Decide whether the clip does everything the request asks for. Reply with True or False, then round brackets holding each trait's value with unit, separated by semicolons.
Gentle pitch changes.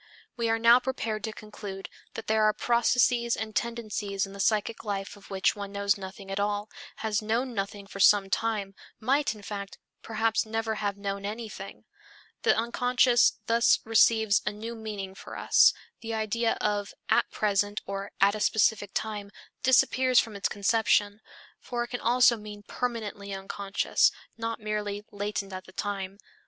True (2.2 semitones)